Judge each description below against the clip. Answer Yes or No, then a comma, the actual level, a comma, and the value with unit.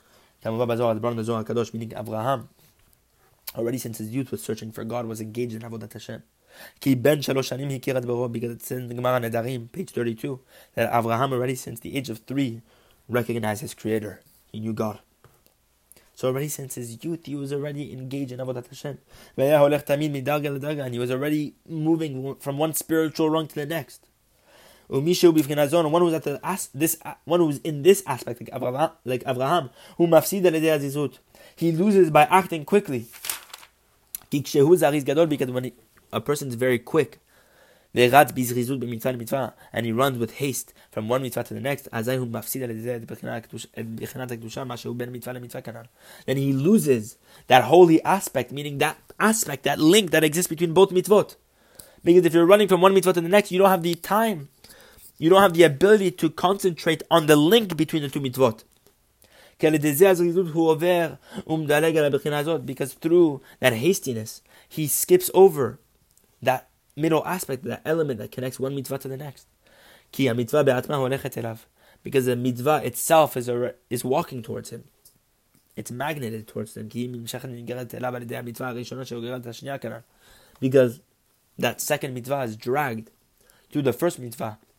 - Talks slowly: Yes, slow, 125 wpm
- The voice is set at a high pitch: No, low, 135 Hz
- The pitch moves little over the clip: No, average, 4.7 semitones